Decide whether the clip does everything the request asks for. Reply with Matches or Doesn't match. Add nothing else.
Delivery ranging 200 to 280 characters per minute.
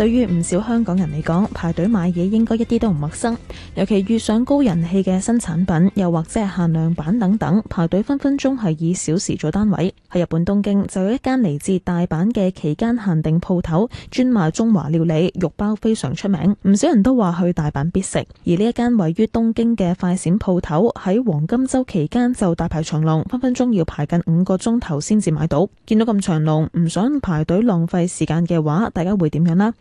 Doesn't match